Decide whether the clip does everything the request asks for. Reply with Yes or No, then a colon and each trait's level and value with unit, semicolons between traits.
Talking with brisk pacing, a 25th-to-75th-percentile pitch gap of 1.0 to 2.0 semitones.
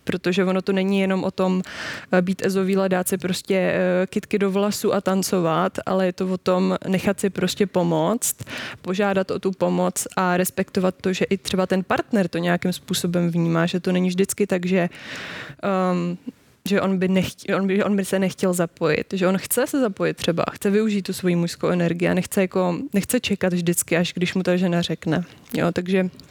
Yes: fast, 195 wpm; narrow, 1.5 semitones